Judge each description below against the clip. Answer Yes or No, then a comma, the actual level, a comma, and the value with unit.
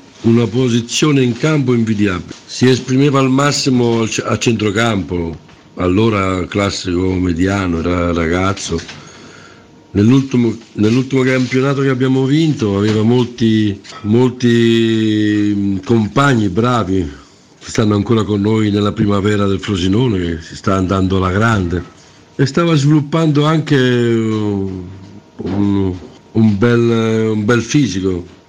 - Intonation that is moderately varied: Yes, average, 4.4 semitones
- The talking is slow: Yes, slow, 110 wpm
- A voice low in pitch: Yes, low, 110 Hz